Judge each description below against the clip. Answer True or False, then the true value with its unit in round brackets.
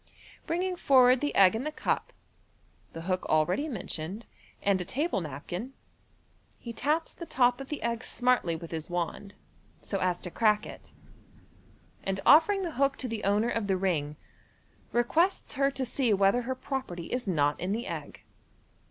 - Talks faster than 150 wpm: True (170 wpm)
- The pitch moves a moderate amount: False (6.7 semitones)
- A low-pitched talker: False (230 Hz)